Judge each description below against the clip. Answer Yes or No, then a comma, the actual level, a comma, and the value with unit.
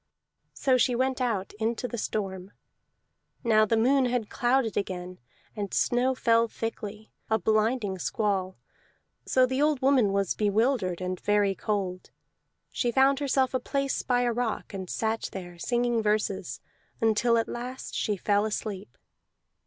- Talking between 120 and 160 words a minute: Yes, average, 145 wpm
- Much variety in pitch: No, average, 3.8 semitones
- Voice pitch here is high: Yes, high, 220 Hz